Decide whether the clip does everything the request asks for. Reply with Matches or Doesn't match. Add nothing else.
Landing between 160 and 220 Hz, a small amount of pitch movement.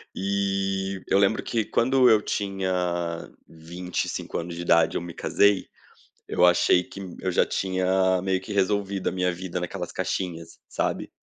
Doesn't match